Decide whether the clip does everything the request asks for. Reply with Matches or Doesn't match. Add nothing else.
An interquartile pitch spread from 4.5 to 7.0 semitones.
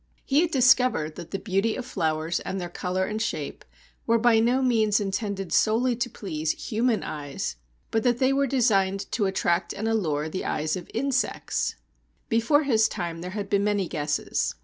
Matches